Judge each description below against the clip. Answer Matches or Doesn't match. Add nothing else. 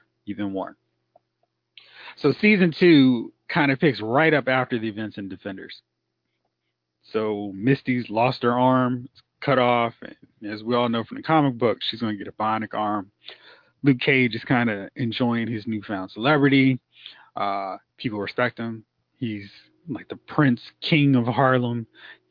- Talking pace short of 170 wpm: Matches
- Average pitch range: Matches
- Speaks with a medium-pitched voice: Doesn't match